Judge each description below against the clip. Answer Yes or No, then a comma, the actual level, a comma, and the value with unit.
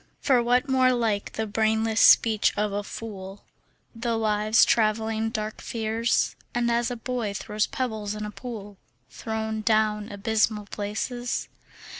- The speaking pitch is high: Yes, high, 220 Hz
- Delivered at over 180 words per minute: No, average, 140 wpm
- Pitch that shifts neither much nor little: No, narrow, 1.8 semitones